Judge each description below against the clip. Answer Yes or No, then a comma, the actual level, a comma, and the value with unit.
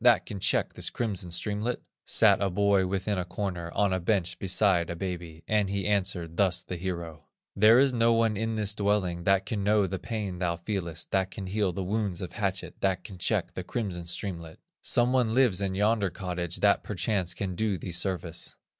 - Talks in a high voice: No, very low, 95 Hz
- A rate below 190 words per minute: No, average, 200 wpm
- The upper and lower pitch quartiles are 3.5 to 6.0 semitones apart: No, average, 2.9 semitones